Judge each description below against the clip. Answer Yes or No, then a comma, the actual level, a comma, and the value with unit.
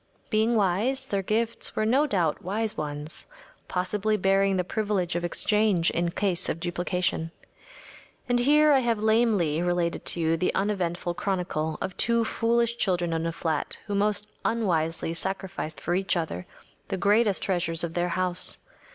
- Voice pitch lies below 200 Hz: Yes, high, 190 Hz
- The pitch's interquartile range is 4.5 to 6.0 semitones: No, average, 4.0 semitones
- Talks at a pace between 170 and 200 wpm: No, average, 160 wpm